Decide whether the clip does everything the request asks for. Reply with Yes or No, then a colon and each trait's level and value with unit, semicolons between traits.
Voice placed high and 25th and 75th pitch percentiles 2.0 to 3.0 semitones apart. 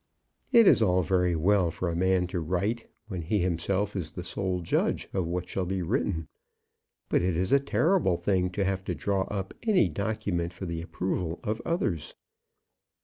No: very low, 95 Hz; narrow, 2.6 semitones